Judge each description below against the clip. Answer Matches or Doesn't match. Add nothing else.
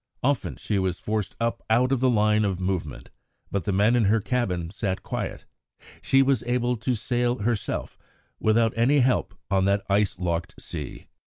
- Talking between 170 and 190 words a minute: Matches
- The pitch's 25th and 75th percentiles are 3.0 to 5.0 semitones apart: Matches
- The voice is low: Matches